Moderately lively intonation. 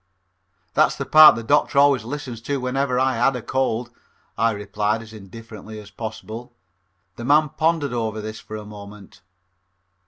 Yes: average, 3.9 semitones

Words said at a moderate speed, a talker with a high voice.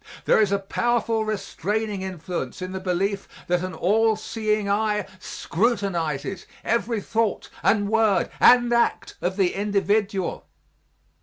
No: slow, 130 wpm; high, 205 Hz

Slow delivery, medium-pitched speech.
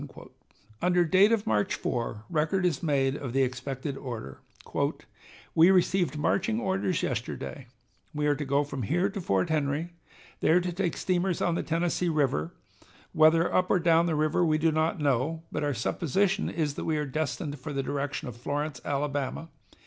No: average, 175 wpm; medium, 155 Hz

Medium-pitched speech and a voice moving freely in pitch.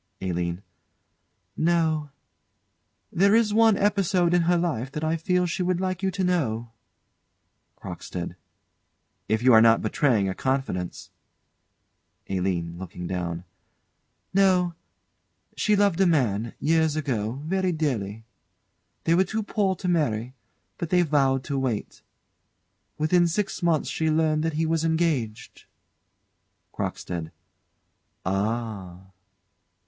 Yes: medium, 155 Hz; wide, 8.3 semitones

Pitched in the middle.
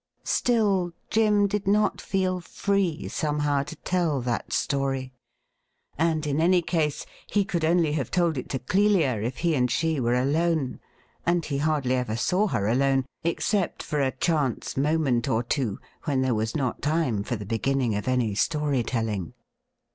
Yes: medium, 145 Hz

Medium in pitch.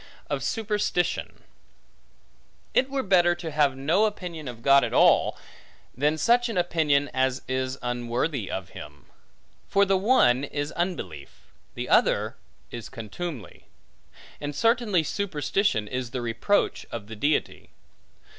Yes: medium, 145 Hz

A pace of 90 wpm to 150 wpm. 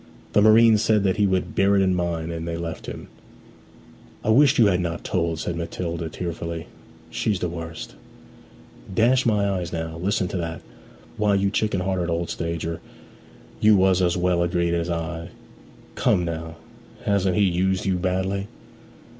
No: average, 165 wpm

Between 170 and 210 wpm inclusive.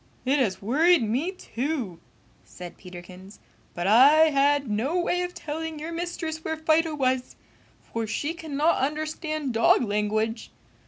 No: average, 140 wpm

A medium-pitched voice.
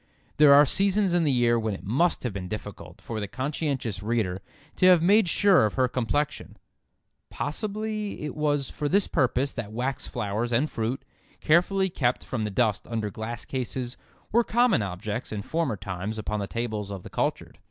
No: low, 125 Hz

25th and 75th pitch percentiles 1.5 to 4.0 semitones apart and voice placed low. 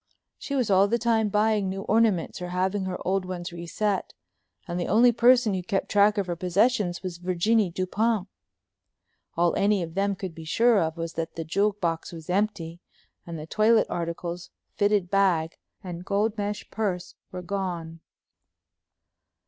No: average, 3.3 semitones; high, 190 Hz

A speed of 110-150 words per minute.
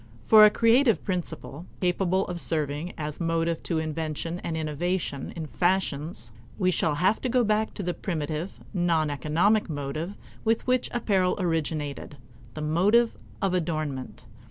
Yes: average, 145 wpm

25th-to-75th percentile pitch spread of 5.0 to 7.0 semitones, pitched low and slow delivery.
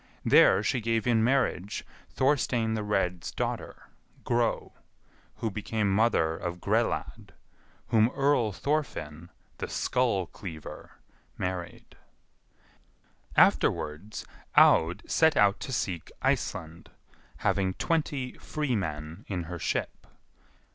Yes: wide, 5.5 semitones; low, 105 Hz; slow, 100 wpm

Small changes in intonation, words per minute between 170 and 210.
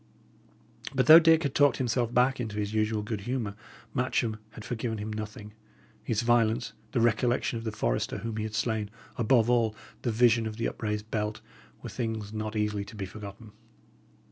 Yes: narrow, 2.1 semitones; average, 180 wpm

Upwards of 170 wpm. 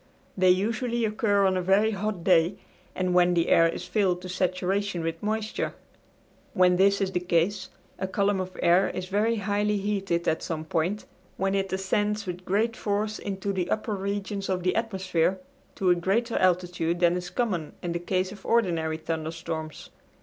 Yes: average, 180 wpm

